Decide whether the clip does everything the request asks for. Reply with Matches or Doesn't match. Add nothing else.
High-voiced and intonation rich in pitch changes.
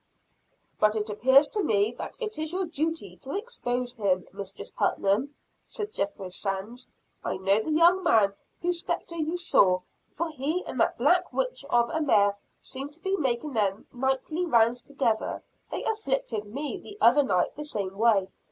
Matches